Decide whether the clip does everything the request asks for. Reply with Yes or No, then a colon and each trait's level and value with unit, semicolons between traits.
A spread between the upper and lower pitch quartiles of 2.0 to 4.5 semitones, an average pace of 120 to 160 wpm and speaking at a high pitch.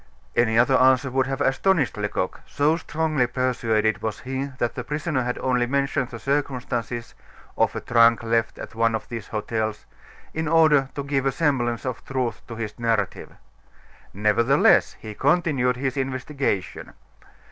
No: average, 3.1 semitones; average, 155 wpm; low, 125 Hz